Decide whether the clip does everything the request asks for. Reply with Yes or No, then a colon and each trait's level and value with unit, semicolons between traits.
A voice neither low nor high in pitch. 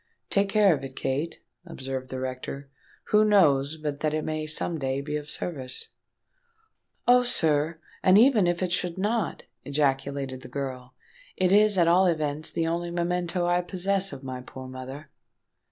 Yes: medium, 155 Hz